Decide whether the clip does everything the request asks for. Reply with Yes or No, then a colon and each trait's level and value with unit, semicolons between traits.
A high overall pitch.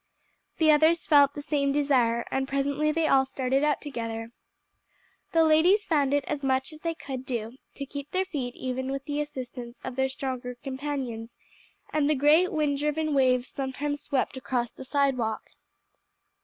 Yes: very high, 275 Hz